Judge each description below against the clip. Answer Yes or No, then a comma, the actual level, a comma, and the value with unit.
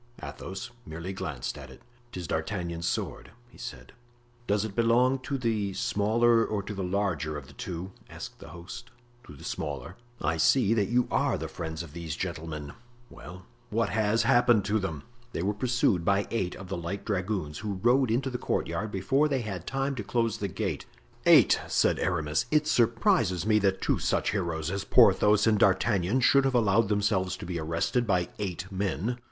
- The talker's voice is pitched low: Yes, low, 100 Hz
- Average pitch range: Yes, average, 4.7 semitones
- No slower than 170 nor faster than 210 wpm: Yes, average, 185 wpm